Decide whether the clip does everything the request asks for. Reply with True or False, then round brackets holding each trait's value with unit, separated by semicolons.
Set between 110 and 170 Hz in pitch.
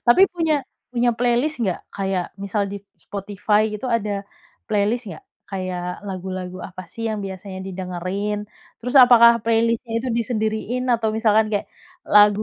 False (210 Hz)